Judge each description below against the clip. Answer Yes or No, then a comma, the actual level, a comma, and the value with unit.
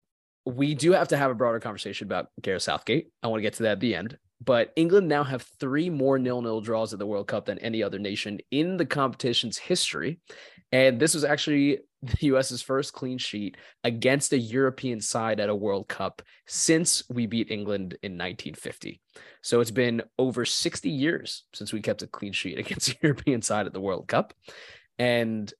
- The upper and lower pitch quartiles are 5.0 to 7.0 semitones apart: No, average, 4.2 semitones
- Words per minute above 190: Yes, average, 200 wpm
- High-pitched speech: No, low, 125 Hz